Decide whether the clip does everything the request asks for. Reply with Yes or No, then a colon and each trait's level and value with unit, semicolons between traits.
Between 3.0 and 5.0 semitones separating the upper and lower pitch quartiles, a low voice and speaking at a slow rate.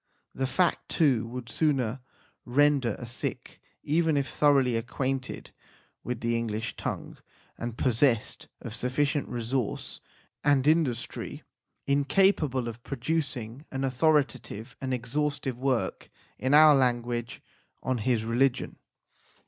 Yes: average, 3.3 semitones; low, 130 Hz; slow, 115 wpm